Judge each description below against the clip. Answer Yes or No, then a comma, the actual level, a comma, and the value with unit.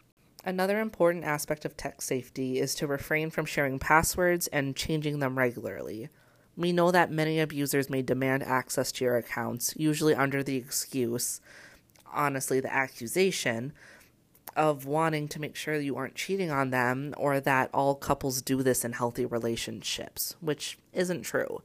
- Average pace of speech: Yes, average, 155 wpm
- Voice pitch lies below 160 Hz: Yes, medium, 140 Hz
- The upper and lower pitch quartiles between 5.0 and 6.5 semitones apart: No, average, 3.2 semitones